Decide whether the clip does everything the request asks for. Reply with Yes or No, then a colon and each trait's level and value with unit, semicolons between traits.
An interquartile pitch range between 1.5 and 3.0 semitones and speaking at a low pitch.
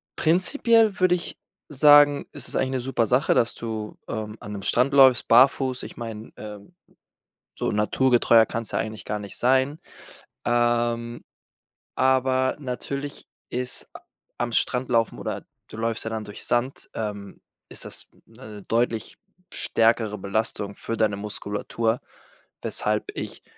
No: average, 3.4 semitones; low, 120 Hz